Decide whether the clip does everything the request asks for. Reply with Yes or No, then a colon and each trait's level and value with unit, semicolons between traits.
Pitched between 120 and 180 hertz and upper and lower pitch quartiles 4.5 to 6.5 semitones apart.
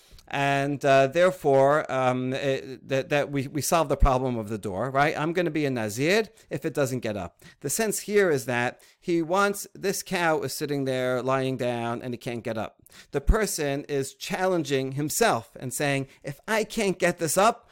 Yes: medium, 140 Hz; average, 4.8 semitones